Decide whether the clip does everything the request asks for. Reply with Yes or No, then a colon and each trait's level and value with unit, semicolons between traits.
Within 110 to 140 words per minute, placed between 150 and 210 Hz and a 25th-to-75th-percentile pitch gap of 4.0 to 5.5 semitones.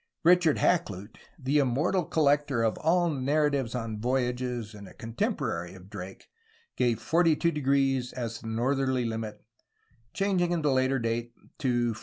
No: slow, 135 wpm; low, 130 Hz; average, 4.5 semitones